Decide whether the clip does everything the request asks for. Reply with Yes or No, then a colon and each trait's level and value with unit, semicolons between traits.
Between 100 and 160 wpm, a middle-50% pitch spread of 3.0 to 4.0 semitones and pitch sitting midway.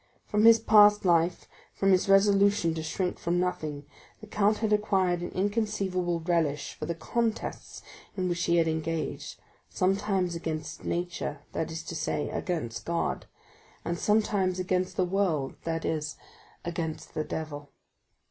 Yes: average, 150 wpm; average, 3.4 semitones; medium, 175 Hz